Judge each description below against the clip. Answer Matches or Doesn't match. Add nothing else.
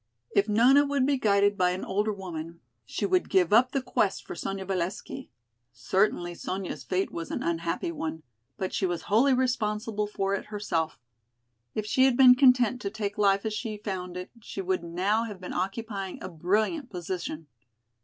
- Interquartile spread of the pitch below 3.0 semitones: Doesn't match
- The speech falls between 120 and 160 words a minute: Doesn't match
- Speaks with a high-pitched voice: Matches